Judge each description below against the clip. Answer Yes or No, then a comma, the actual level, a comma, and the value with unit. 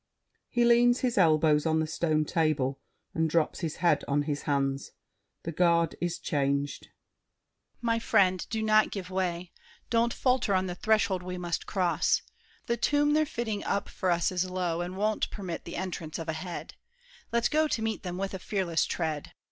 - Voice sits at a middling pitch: Yes, medium, 180 Hz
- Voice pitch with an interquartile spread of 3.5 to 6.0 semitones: Yes, average, 5.0 semitones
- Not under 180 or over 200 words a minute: Yes, average, 185 wpm